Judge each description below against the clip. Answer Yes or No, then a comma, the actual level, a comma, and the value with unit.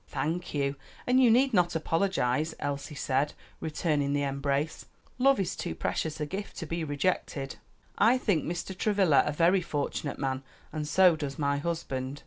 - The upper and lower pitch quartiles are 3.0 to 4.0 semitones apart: No, average, 4.4 semitones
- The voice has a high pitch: No, medium, 155 Hz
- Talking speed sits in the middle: Yes, average, 165 wpm